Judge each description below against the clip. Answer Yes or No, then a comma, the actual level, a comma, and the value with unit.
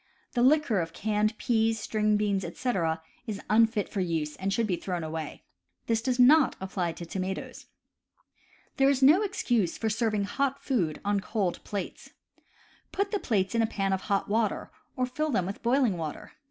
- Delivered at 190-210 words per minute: No, average, 180 wpm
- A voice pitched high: Yes, high, 210 Hz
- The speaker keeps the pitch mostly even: No, average, 4.4 semitones